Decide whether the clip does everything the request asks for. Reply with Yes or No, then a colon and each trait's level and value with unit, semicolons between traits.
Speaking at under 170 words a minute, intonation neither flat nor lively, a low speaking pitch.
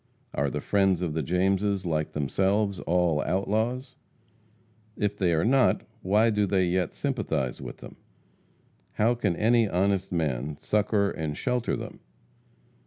Yes: average, 140 wpm; average, 4.1 semitones; very low, 95 Hz